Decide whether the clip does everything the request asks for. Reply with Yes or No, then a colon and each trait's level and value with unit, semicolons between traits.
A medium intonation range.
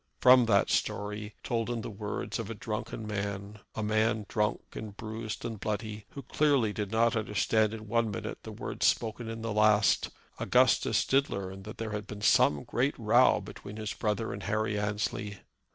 No: narrow, 1.4 semitones